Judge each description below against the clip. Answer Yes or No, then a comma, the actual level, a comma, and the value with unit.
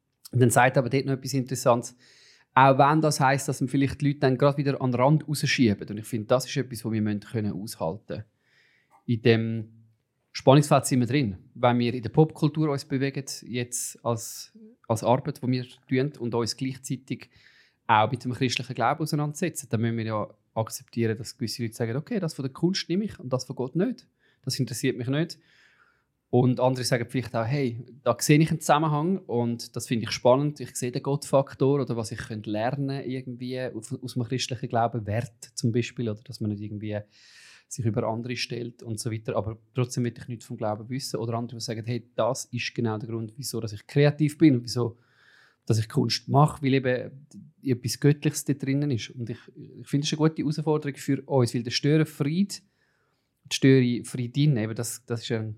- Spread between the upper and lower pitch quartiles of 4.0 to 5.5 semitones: No, average, 3.1 semitones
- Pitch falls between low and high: No, low, 125 Hz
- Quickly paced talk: Yes, fast, 205 wpm